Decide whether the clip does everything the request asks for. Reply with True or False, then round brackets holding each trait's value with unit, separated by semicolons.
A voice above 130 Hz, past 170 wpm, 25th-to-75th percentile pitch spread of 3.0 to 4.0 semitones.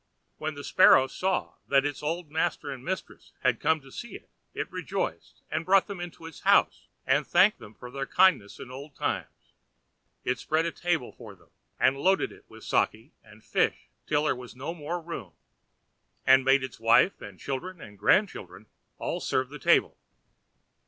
False (140 Hz; 180 wpm; 4.9 semitones)